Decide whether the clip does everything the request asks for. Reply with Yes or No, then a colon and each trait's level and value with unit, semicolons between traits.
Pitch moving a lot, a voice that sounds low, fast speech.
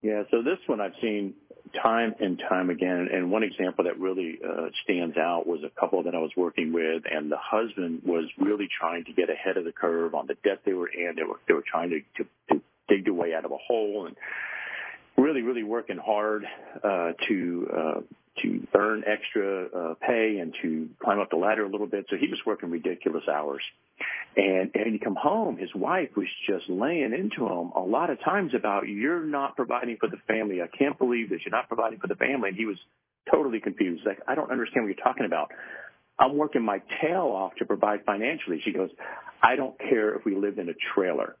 Yes: wide, 7.5 semitones; low, 105 Hz; fast, 220 wpm